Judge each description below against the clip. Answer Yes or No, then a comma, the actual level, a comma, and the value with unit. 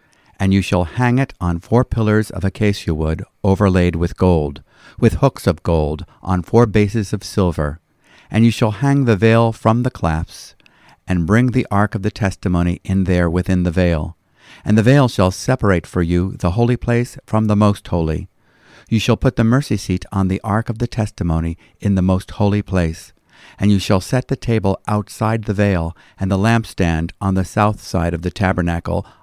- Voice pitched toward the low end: Yes, low, 100 Hz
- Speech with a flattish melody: No, average, 4.0 semitones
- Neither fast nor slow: Yes, average, 195 wpm